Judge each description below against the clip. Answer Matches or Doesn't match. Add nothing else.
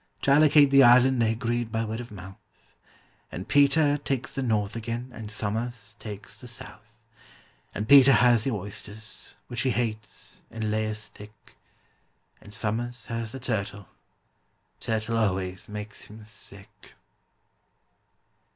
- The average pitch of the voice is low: Matches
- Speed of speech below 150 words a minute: Matches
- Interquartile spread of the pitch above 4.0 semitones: Doesn't match